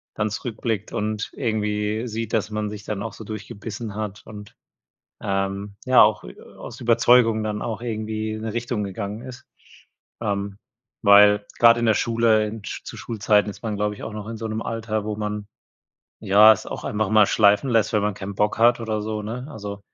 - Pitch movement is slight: Yes, narrow, 1.6 semitones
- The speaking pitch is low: Yes, low, 110 Hz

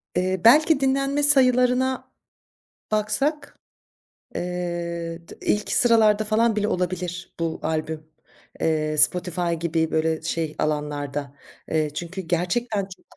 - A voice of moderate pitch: Yes, medium, 180 Hz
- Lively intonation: Yes, wide, 6.0 semitones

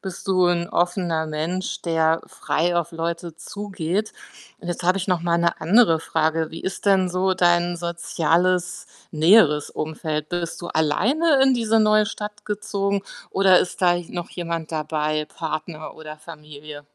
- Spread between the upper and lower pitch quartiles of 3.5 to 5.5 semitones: No, average, 2.9 semitones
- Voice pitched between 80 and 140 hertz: No, medium, 175 Hz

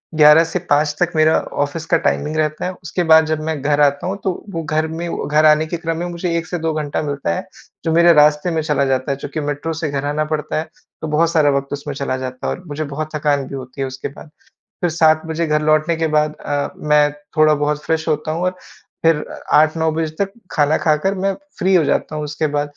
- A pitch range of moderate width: No, narrow, 1.8 semitones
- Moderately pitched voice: Yes, medium, 155 Hz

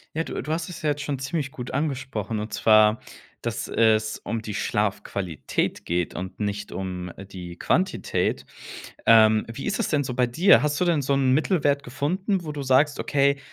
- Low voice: Yes, low, 130 Hz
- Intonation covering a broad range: Yes, wide, 5.7 semitones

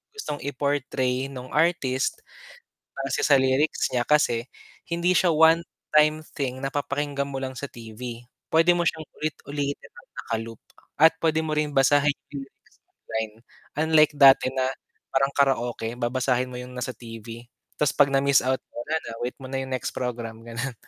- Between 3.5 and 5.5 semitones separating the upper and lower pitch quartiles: No, average, 3.1 semitones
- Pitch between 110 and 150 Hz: Yes, low, 135 Hz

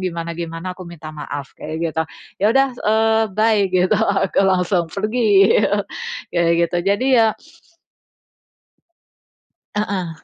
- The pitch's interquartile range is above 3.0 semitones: Yes, average, 4.2 semitones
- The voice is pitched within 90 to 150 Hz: No, medium, 185 Hz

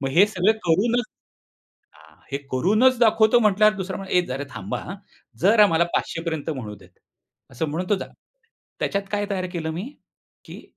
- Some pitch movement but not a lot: Yes, average, 4.9 semitones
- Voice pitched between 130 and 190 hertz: Yes, medium, 185 Hz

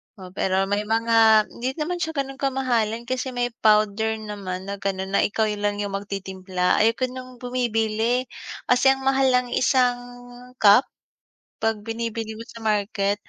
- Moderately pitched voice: No, high, 225 Hz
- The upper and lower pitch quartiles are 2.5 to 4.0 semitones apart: Yes, average, 3.5 semitones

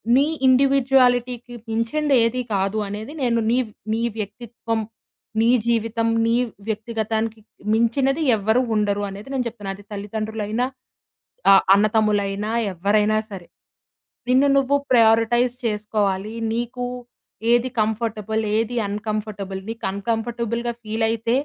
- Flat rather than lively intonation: Yes, narrow, 2.3 semitones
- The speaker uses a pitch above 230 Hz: No, high, 225 Hz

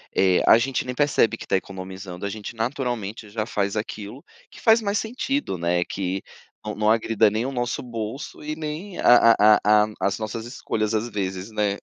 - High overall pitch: No, low, 110 Hz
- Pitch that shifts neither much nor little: Yes, average, 3.7 semitones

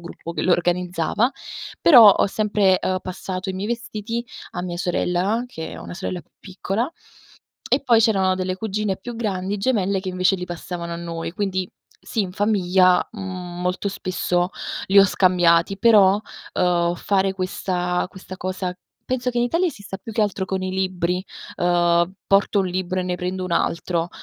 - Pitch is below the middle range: No, medium, 185 Hz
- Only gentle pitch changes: Yes, narrow, 2.2 semitones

